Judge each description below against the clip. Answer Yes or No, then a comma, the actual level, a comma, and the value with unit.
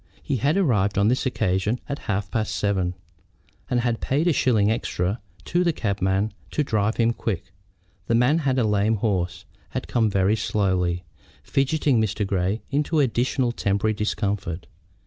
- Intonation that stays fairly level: No, average, 4.3 semitones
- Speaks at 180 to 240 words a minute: No, average, 160 wpm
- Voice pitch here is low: Yes, low, 110 Hz